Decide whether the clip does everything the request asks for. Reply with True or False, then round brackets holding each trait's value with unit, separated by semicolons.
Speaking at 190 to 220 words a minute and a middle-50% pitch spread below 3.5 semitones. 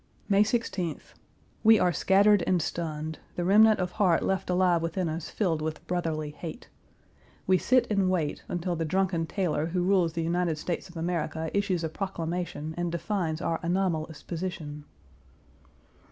False (155 wpm; 2.7 semitones)